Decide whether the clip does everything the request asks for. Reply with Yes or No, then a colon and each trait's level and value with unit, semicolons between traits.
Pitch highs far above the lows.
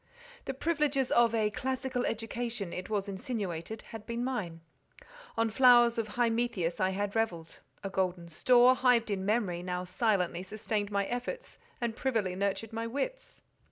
No: average, 4.2 semitones